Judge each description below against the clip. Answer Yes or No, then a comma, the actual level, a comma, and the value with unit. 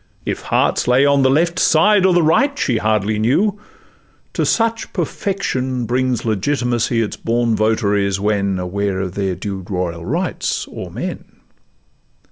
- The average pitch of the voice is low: Yes, low, 120 Hz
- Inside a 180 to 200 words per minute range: No, average, 145 wpm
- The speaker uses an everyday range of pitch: No, wide, 7.0 semitones